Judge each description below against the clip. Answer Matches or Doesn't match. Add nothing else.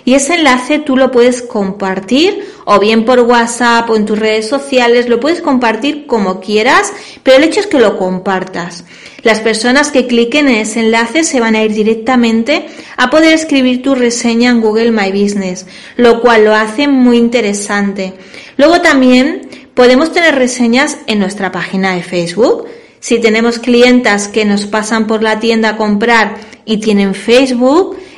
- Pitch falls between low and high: Doesn't match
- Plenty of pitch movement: Doesn't match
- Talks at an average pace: Matches